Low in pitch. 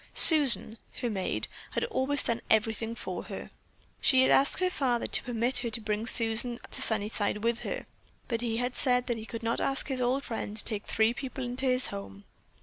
No: high, 235 Hz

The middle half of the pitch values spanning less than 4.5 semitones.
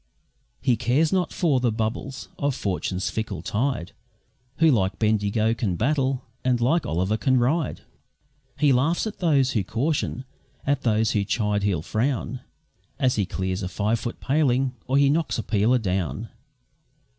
No: average, 4.8 semitones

